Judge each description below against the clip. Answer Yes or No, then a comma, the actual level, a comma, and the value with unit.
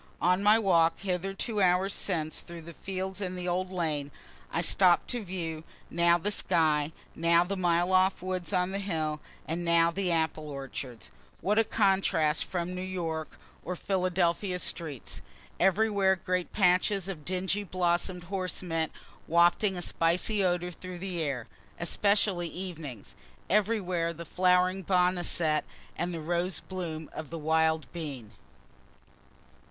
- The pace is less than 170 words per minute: Yes, average, 145 wpm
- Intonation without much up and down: Yes, narrow, 2.3 semitones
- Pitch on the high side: No, medium, 180 Hz